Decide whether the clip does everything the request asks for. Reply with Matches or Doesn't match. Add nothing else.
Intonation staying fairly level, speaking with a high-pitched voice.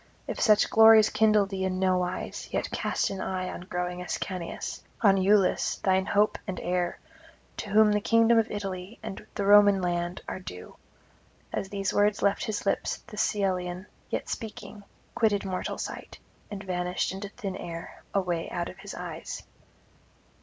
Matches